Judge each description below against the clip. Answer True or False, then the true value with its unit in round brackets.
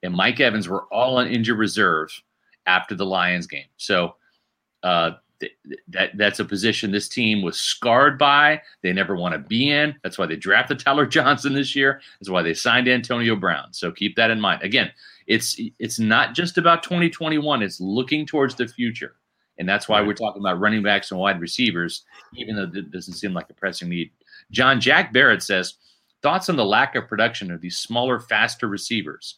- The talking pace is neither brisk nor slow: True (195 wpm)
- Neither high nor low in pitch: False (110 Hz)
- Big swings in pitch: True (5.7 semitones)